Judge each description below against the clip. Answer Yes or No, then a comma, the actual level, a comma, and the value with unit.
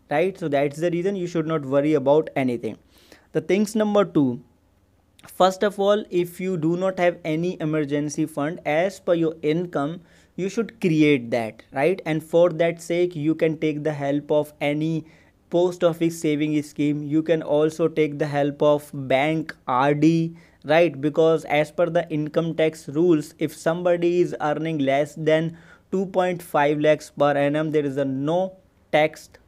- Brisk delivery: No, average, 175 wpm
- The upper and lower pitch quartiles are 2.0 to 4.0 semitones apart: Yes, average, 2.8 semitones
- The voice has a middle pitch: Yes, medium, 155 Hz